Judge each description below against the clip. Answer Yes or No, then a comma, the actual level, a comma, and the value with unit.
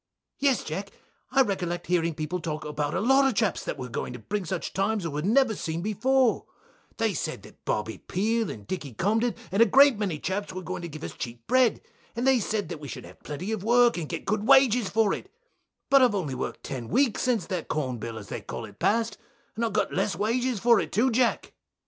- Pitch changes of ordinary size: No, wide, 6.5 semitones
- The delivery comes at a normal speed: No, fast, 235 wpm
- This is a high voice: Yes, high, 200 Hz